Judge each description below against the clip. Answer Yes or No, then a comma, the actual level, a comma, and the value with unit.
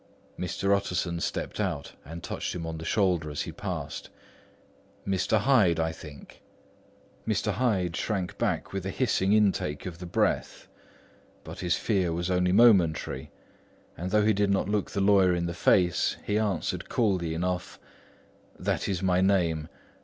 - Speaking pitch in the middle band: No, very low, 90 Hz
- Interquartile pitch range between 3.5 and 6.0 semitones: No, average, 2.9 semitones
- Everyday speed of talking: Yes, average, 160 wpm